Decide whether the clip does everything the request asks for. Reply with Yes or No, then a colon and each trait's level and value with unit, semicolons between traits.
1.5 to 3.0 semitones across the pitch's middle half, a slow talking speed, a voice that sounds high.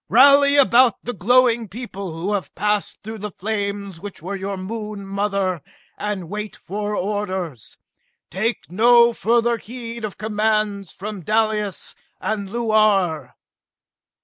Yes: narrow, 2.5 semitones; slow, 125 wpm; high, 210 Hz